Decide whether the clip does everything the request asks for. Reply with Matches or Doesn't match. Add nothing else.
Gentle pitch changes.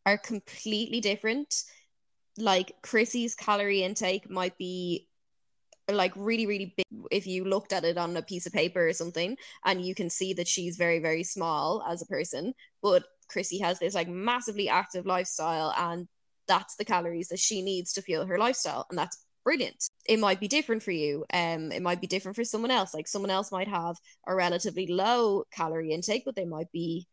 Doesn't match